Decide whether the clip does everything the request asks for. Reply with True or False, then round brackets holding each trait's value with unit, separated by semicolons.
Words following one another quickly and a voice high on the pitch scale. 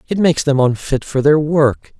False (210 wpm; 145 Hz)